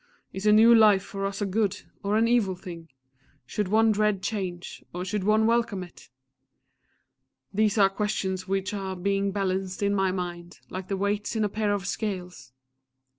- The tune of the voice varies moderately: No, narrow, 2.1 semitones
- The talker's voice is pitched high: Yes, high, 195 Hz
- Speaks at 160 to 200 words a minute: Yes, average, 180 wpm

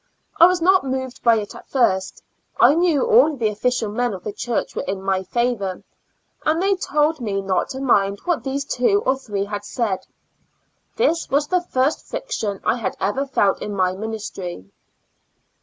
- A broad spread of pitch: Yes, wide, 6.9 semitones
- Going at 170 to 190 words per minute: Yes, average, 180 wpm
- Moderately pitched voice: No, high, 245 Hz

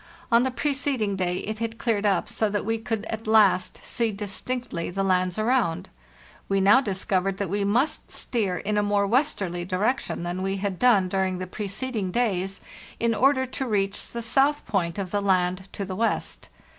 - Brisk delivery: No, average, 190 wpm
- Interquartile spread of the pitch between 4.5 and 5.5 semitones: No, average, 3.5 semitones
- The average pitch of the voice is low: No, high, 205 Hz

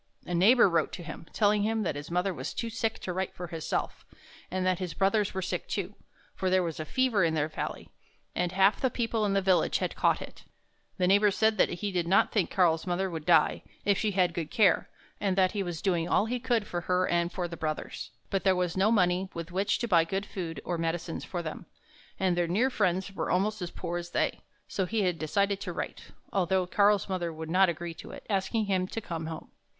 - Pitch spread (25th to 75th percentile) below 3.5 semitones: Yes, average, 2.8 semitones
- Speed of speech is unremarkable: No, fast, 235 wpm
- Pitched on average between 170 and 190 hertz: Yes, medium, 185 Hz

